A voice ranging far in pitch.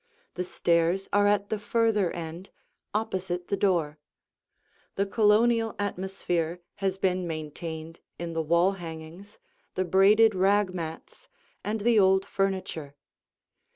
No: average, 3.2 semitones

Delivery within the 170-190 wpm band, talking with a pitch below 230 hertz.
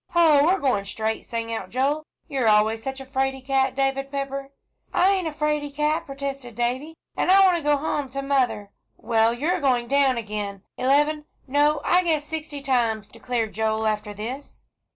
No: average, 185 wpm; very high, 270 Hz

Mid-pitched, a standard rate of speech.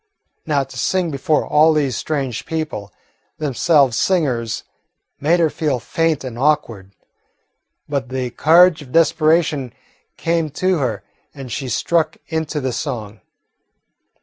No: medium, 150 Hz; slow, 125 wpm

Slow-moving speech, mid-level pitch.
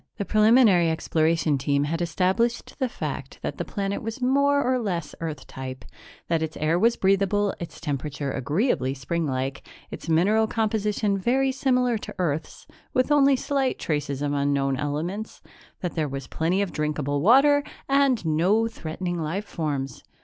No: average, 155 wpm; medium, 175 Hz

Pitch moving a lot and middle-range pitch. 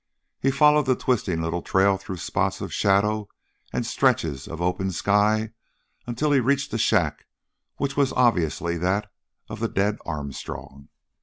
No: wide, 5.9 semitones; low, 100 Hz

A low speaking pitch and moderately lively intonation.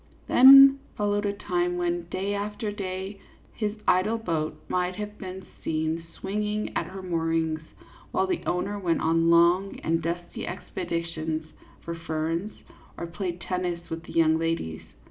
No: medium, 175 Hz; average, 3.5 semitones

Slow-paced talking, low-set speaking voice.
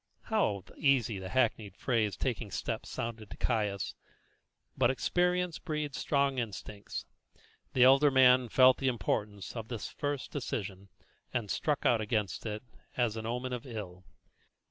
No: average, 145 wpm; low, 120 Hz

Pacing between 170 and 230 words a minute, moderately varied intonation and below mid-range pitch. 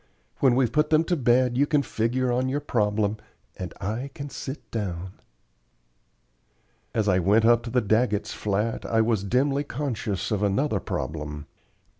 No: average, 160 wpm; average, 4.2 semitones; low, 115 Hz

